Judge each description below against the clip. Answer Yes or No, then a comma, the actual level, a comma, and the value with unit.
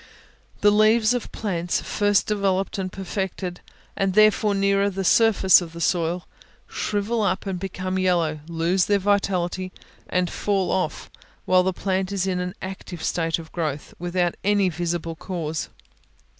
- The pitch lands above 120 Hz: Yes, medium, 185 Hz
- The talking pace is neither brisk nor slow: Yes, average, 150 wpm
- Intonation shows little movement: Yes, narrow, 2.3 semitones